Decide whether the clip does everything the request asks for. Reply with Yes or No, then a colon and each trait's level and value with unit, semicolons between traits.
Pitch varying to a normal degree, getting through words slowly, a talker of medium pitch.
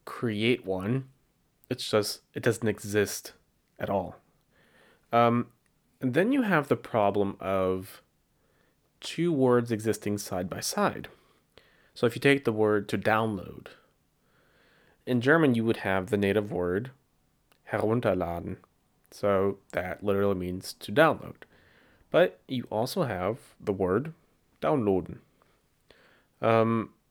No: average, 3.8 semitones; slow, 120 wpm; low, 110 Hz